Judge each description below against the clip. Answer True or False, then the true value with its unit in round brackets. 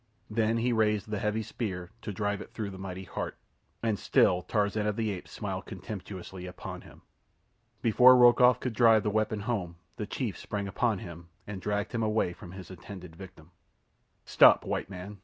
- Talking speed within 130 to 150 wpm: False (180 wpm)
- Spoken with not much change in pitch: False (3.0 semitones)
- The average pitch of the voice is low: True (105 Hz)